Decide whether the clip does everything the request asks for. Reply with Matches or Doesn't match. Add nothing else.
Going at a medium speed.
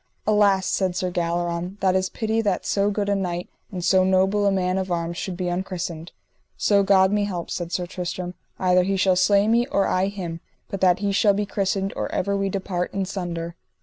Doesn't match